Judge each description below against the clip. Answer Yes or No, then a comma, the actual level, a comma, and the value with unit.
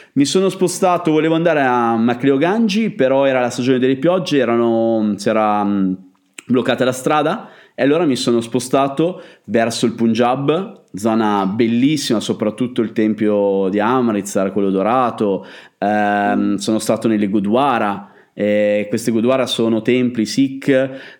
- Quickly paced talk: No, average, 130 wpm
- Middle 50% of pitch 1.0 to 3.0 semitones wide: No, average, 4.4 semitones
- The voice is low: Yes, low, 120 Hz